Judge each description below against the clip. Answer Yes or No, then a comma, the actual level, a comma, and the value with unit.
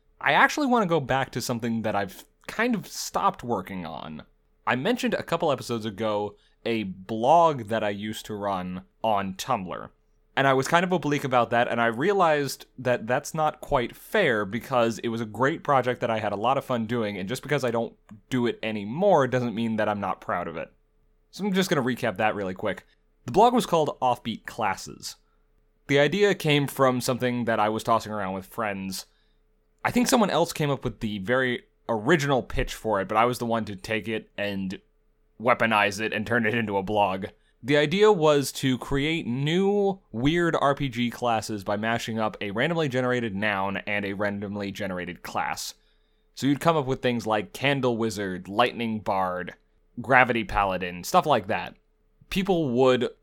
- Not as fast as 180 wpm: No, average, 195 wpm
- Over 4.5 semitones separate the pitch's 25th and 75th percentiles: Yes, average, 5.3 semitones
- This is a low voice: Yes, low, 120 Hz